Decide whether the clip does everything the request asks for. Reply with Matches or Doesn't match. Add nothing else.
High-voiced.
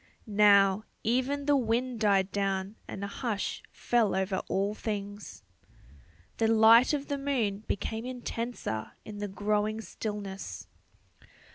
Matches